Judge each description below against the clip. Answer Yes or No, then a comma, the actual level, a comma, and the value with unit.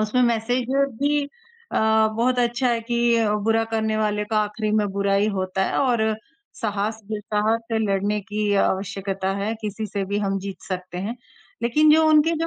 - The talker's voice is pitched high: Yes, high, 220 Hz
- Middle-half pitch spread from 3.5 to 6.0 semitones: No, average, 3.0 semitones